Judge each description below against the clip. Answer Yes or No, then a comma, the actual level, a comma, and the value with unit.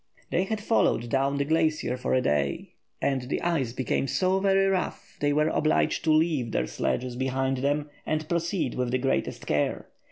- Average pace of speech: Yes, average, 185 wpm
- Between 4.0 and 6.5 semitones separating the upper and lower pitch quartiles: Yes, average, 4.5 semitones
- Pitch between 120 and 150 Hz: Yes, medium, 140 Hz